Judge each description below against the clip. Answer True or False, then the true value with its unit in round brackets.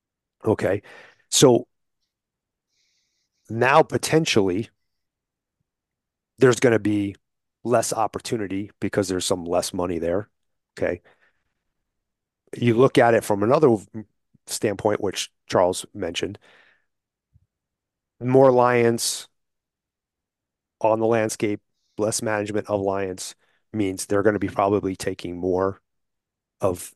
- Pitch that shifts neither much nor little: True (3.2 semitones)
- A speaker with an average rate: False (100 wpm)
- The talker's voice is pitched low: True (105 Hz)